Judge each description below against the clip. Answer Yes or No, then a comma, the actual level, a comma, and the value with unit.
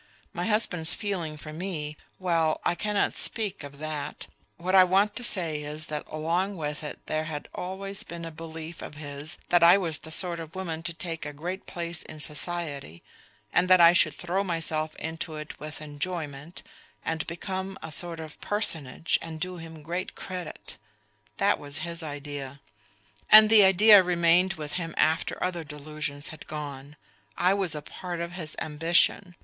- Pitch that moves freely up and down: No, average, 3.0 semitones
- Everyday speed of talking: Yes, average, 175 wpm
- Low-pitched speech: No, medium, 165 Hz